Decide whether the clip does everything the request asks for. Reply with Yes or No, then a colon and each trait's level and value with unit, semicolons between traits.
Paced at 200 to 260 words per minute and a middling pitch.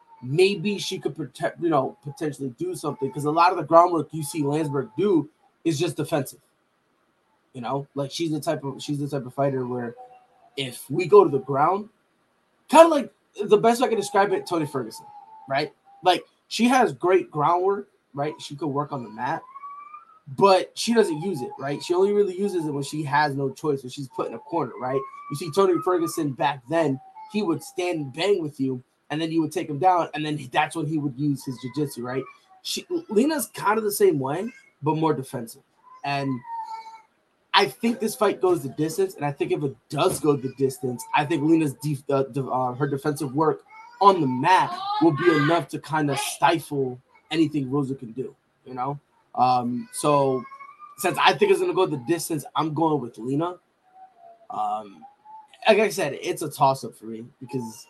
Yes: fast, 205 wpm; medium, 160 Hz